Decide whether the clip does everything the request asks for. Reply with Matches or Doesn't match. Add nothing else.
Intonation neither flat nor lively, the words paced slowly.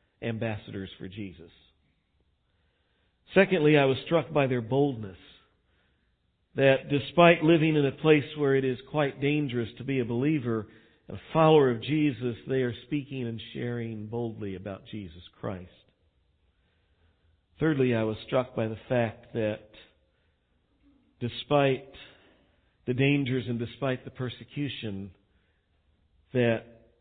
Doesn't match